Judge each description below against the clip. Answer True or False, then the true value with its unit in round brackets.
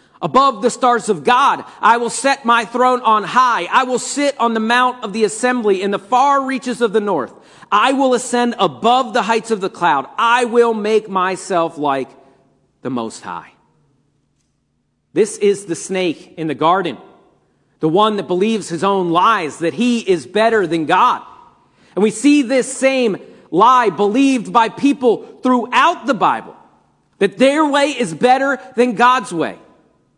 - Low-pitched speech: False (230 Hz)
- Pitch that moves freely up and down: False (4.6 semitones)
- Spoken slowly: False (170 wpm)